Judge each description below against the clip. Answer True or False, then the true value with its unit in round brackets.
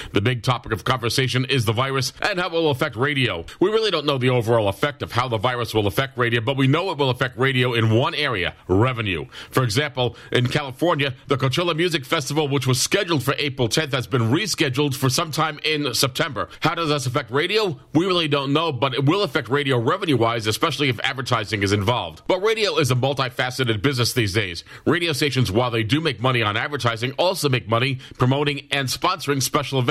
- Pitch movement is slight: False (3.3 semitones)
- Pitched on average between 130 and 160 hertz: True (135 Hz)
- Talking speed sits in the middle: False (215 wpm)